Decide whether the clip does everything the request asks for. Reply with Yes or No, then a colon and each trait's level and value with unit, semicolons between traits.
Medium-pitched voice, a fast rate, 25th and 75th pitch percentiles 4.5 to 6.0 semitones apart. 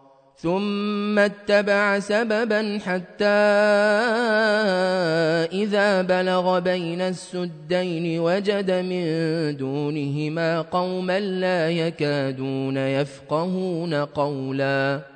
No: medium, 180 Hz; slow, 65 wpm; average, 5.0 semitones